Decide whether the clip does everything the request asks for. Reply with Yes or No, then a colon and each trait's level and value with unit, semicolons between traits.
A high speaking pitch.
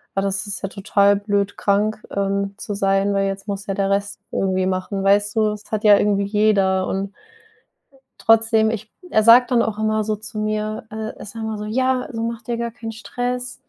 Yes: high, 210 Hz